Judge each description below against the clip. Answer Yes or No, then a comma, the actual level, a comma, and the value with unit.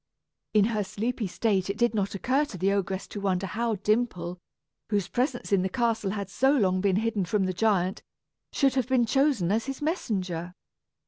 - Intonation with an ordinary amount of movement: Yes, average, 4.0 semitones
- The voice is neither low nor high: No, high, 205 Hz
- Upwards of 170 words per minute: Yes, average, 190 wpm